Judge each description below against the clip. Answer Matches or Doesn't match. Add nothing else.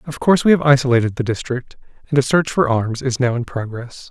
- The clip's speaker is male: Matches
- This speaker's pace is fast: Matches